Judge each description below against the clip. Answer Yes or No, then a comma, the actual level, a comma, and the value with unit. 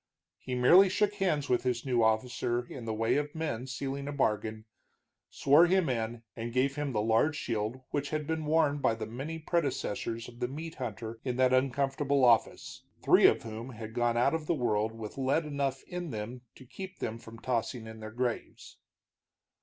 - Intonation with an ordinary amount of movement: Yes, average, 4.3 semitones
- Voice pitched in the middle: No, low, 125 Hz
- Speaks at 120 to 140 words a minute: No, average, 195 wpm